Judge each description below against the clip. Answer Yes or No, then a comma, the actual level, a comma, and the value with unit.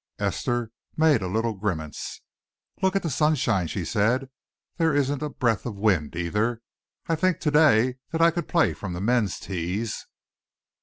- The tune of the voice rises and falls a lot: Yes, wide, 7.2 semitones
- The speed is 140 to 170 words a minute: Yes, average, 165 wpm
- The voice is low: Yes, low, 115 Hz